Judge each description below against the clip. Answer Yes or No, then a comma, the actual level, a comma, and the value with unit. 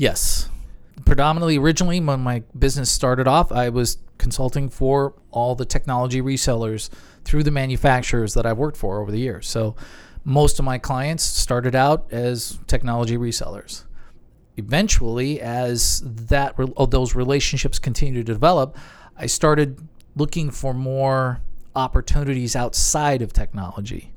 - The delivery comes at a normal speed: No, slow, 130 wpm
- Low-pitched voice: Yes, low, 130 Hz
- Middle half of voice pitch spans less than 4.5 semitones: Yes, average, 2.9 semitones